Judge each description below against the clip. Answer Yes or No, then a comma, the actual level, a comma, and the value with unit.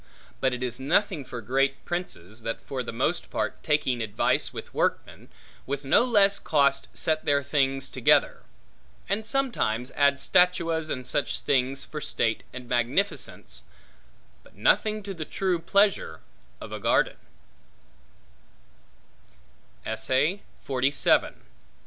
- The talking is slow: Yes, slow, 120 wpm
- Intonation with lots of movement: Yes, wide, 5.8 semitones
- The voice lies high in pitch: No, medium, 140 Hz